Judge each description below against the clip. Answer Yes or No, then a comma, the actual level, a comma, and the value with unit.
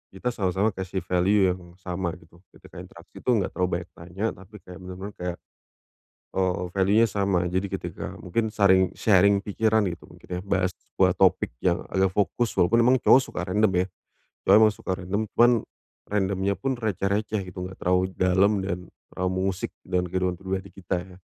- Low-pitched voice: Yes, very low, 95 Hz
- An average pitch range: No, narrow, 1.9 semitones